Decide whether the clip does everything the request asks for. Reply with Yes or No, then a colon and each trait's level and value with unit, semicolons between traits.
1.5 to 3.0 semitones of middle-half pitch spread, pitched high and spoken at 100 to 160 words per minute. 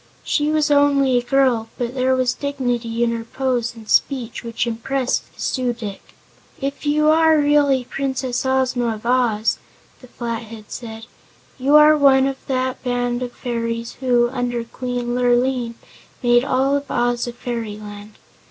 Yes: narrow, 2.4 semitones; high, 245 Hz; average, 150 wpm